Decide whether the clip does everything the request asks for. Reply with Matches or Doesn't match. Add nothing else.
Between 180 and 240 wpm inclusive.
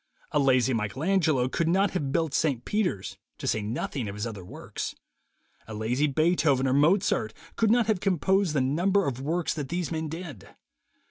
Matches